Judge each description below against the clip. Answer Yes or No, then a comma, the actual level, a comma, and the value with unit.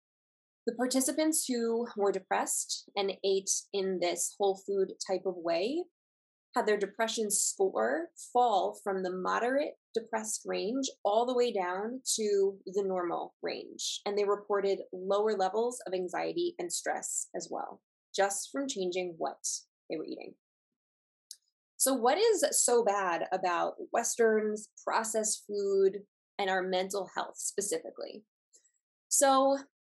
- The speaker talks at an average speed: No, slow, 130 wpm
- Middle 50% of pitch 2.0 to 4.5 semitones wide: No, average, 5.3 semitones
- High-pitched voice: Yes, high, 210 Hz